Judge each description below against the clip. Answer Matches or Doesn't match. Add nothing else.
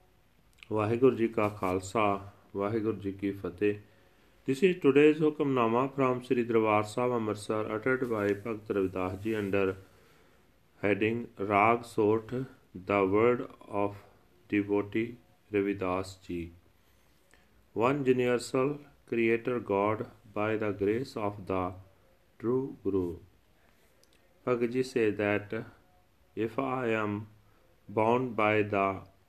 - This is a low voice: Matches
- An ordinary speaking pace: Matches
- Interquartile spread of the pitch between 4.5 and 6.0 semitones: Doesn't match